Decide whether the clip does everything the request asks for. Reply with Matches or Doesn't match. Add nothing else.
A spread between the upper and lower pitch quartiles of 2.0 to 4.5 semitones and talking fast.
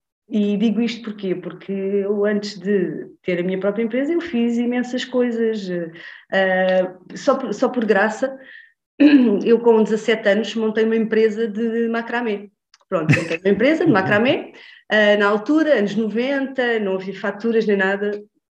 Doesn't match